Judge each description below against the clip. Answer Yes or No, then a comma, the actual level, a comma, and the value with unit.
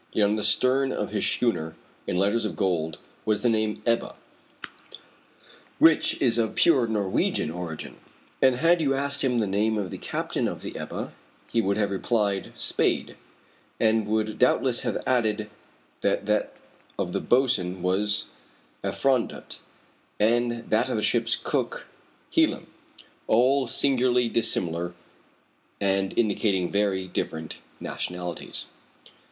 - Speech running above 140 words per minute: No, slow, 135 wpm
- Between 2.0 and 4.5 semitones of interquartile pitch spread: Yes, average, 4.0 semitones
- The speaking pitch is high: No, low, 110 Hz